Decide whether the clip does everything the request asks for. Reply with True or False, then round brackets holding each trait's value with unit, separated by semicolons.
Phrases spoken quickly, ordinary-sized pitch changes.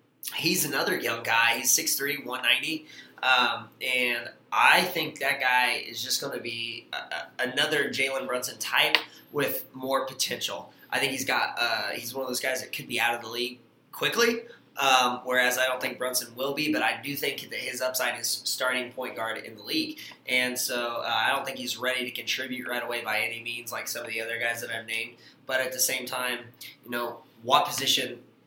False (210 wpm; 1.8 semitones)